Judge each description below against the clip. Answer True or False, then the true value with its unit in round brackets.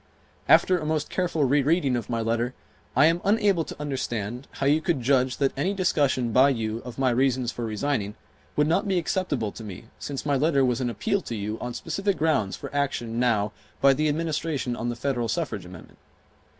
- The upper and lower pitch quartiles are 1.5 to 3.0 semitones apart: False (4.7 semitones)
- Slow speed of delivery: False (200 wpm)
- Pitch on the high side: False (135 Hz)